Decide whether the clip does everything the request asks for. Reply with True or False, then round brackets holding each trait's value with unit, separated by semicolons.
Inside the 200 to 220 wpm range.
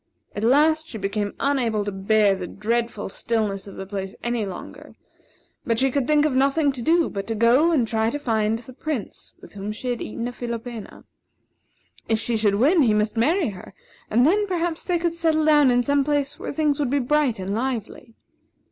True (205 wpm)